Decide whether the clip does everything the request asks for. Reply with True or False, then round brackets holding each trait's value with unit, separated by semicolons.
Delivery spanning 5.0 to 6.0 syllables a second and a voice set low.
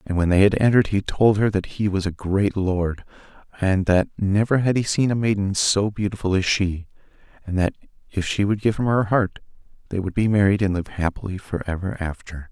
True (5.3 syllables/s; 100 Hz)